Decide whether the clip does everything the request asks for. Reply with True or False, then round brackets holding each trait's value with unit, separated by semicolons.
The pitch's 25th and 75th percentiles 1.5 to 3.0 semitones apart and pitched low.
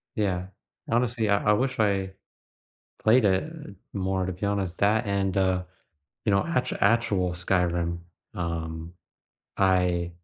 True (2.7 semitones; 95 Hz)